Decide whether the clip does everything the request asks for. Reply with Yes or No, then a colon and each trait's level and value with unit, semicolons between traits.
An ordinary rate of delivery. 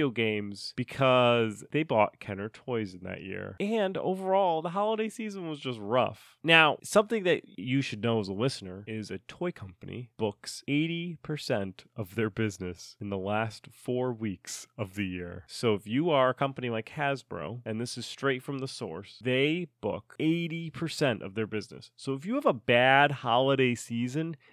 Yes: average, 175 wpm